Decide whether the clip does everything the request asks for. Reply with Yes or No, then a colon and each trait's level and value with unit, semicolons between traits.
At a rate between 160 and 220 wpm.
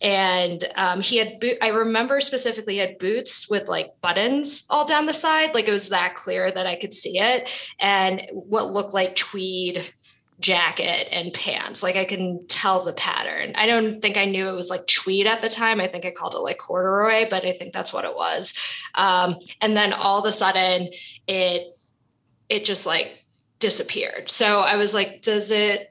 Yes: average, 200 wpm